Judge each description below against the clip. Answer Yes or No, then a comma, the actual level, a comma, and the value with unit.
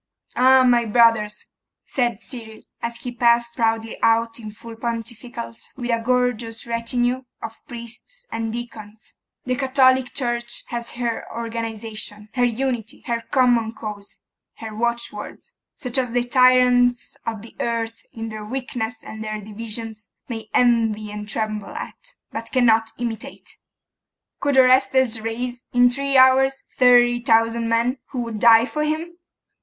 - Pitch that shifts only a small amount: Yes, narrow, 1.8 semitones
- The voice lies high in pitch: Yes, high, 235 Hz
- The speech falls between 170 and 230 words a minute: No, average, 140 wpm